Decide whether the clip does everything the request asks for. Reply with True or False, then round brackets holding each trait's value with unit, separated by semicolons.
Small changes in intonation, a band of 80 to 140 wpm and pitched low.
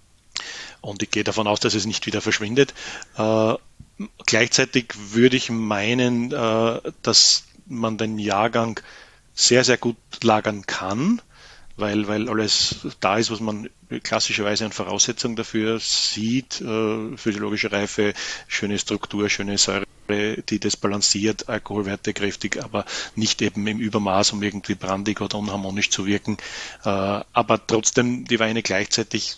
True (1.7 semitones; 135 wpm; 110 Hz)